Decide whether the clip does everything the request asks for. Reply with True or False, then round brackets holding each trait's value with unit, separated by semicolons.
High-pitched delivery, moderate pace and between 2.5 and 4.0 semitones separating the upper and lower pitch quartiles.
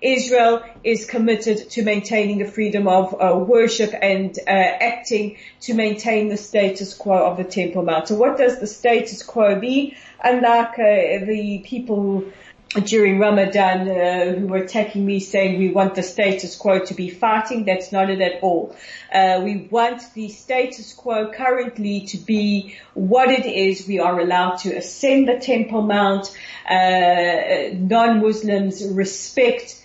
True (205 Hz; 155 wpm; 3.3 semitones)